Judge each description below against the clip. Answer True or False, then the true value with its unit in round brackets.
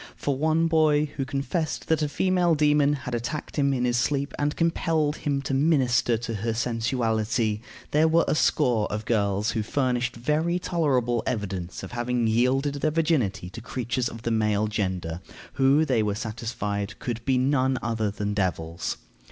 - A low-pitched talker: True (125 Hz)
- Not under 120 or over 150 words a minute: False (170 wpm)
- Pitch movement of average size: True (5.0 semitones)